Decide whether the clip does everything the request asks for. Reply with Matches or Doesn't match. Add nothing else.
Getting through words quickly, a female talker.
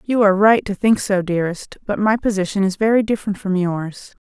Matches